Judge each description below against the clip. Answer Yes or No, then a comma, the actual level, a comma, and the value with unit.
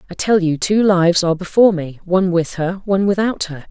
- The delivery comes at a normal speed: No, fast, 225 wpm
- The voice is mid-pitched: Yes, medium, 180 Hz